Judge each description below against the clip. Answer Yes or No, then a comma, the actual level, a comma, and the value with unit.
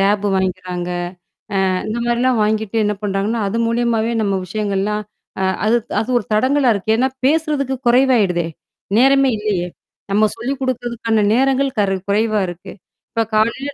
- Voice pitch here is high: Yes, high, 220 Hz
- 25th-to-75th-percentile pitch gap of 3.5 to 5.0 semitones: Yes, average, 3.8 semitones